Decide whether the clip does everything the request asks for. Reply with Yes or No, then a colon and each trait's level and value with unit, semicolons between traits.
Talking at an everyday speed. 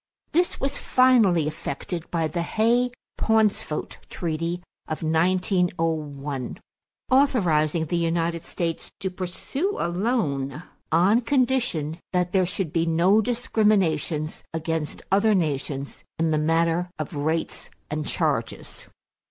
No: slow, 110 wpm